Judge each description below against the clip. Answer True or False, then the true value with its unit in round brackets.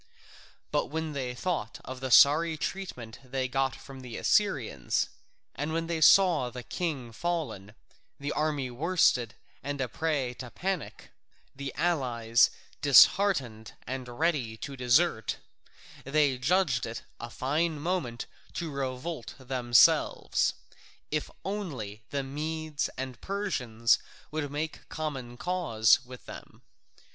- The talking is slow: True (125 wpm)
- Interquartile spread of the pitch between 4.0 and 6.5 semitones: True (4.6 semitones)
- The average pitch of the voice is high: False (135 Hz)